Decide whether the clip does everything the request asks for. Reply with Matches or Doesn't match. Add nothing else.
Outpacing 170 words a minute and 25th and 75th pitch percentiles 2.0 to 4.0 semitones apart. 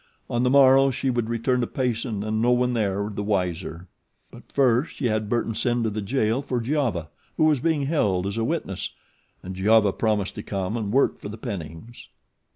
Matches